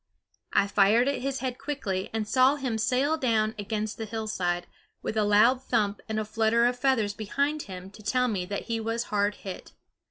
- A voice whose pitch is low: No, high, 220 Hz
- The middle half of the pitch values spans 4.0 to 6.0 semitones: No, average, 3.5 semitones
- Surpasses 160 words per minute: Yes, average, 195 wpm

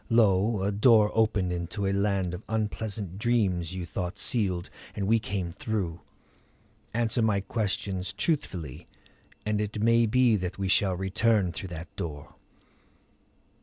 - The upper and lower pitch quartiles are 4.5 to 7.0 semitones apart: No, average, 3.3 semitones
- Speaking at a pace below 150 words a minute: Yes, average, 140 wpm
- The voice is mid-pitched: No, low, 100 Hz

